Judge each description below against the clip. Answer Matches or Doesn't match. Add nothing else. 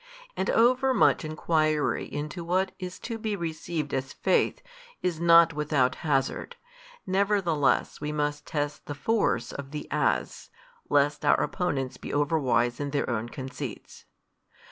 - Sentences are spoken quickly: Doesn't match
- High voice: Doesn't match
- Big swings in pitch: Doesn't match